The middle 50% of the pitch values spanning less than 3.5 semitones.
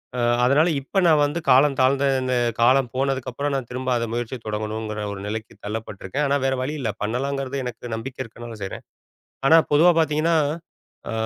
No: average, 3.8 semitones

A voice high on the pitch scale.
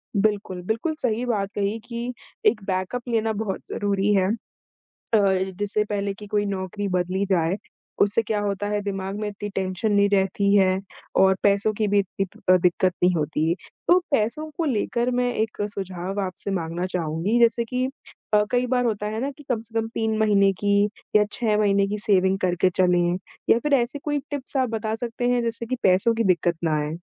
Yes: high, 205 Hz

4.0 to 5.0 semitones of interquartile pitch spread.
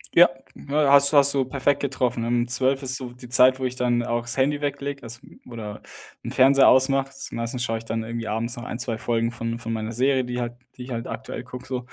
No: narrow, 2.4 semitones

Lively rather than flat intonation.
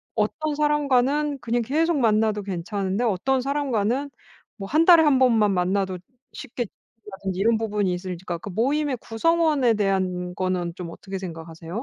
Yes: wide, 6.5 semitones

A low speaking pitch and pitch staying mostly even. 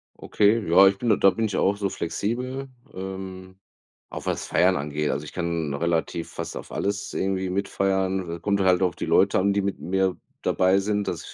Yes: very low, 95 Hz; narrow, 2.0 semitones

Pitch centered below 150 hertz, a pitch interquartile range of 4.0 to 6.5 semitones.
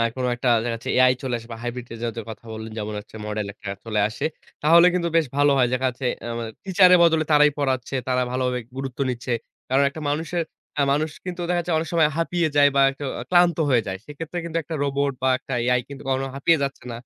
Yes: low, 135 Hz; average, 4.7 semitones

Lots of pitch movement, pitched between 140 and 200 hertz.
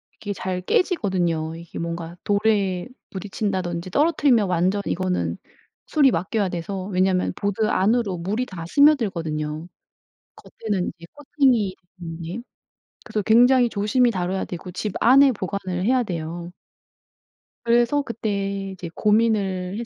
No: average, 4.3 semitones; high, 195 Hz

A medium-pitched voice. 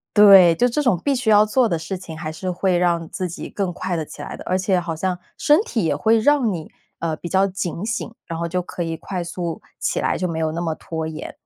Yes: medium, 180 Hz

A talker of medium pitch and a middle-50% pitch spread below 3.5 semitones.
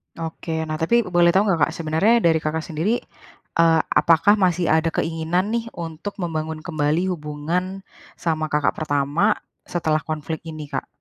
Yes: medium, 165 Hz; narrow, 2.6 semitones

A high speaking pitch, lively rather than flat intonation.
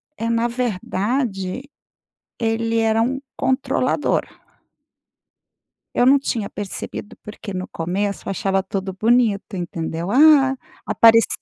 No: high, 225 Hz; average, 4.3 semitones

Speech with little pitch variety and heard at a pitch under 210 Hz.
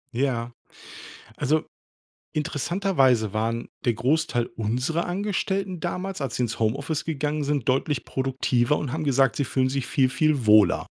No: average, 4.4 semitones; low, 135 Hz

